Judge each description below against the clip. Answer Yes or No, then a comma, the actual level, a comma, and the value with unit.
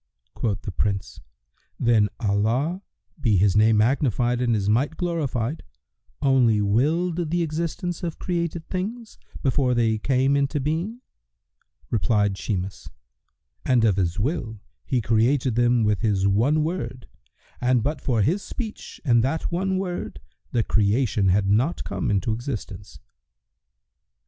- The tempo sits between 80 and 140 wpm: Yes, slow, 135 wpm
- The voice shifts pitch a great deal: Yes, wide, 6.6 semitones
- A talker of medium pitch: No, low, 120 Hz